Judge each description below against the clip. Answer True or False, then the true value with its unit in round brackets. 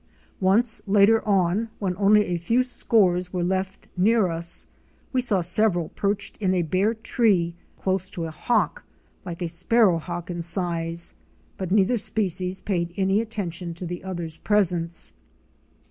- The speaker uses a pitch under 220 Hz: True (185 Hz)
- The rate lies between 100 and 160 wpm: True (150 wpm)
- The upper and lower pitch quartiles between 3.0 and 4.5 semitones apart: True (3.3 semitones)